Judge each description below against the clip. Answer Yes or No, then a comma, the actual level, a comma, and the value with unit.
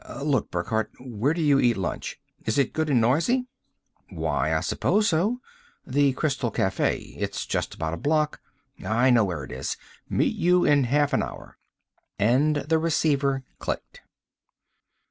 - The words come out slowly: No, average, 160 wpm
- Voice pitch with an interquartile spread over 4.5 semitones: Yes, average, 5.3 semitones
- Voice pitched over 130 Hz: Yes, medium, 140 Hz